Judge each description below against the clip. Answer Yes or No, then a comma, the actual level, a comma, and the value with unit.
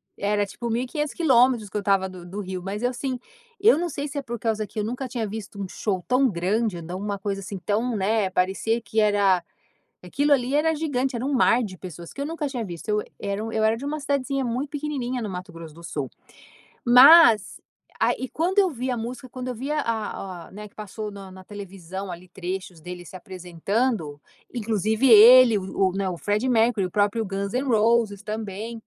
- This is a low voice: No, high, 215 Hz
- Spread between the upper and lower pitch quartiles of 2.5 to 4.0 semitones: No, average, 4.6 semitones